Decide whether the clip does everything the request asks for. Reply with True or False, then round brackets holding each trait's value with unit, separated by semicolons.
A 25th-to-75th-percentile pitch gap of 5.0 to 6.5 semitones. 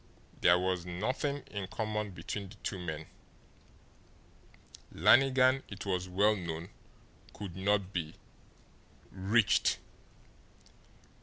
False (3.1 semitones)